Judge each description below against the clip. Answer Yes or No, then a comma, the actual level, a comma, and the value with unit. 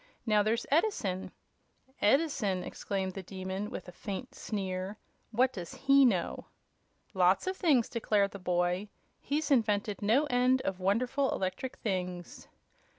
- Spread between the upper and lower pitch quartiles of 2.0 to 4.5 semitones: No, wide, 5.4 semitones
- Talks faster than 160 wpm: No, average, 140 wpm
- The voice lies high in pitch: Yes, high, 210 Hz